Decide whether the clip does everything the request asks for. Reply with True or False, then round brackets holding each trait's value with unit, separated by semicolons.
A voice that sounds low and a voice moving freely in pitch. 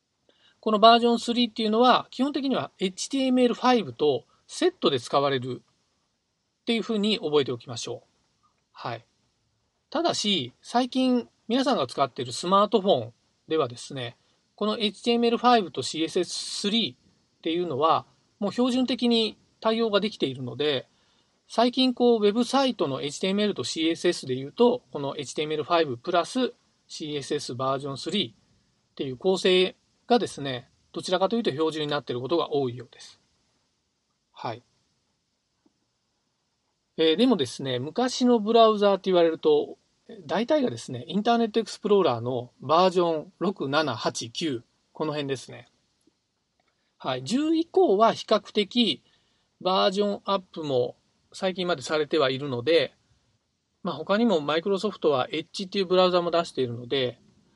False (190 Hz; 8.4 semitones)